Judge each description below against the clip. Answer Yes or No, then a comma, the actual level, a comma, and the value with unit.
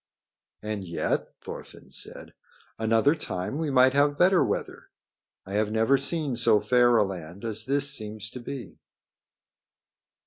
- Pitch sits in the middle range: No, low, 115 Hz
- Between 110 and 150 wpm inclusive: Yes, average, 140 wpm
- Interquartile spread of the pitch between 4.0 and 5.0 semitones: Yes, average, 4.7 semitones